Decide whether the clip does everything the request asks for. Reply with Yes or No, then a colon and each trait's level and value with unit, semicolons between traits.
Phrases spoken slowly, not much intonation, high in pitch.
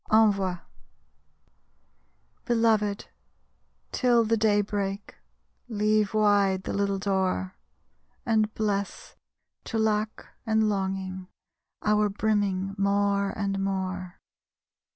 Yes: slow, 90 wpm; narrow, 1.8 semitones; high, 205 Hz